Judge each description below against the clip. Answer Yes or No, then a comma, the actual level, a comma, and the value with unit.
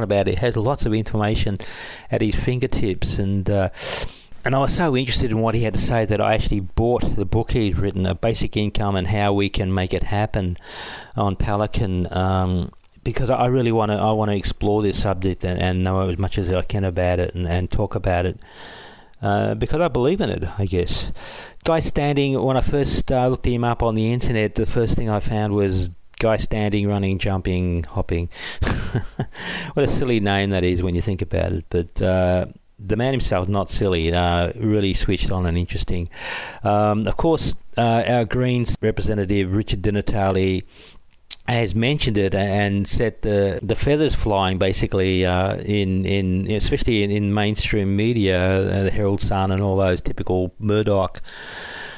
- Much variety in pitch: No, average, 3.2 semitones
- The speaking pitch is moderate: No, low, 100 Hz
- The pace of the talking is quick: No, average, 185 wpm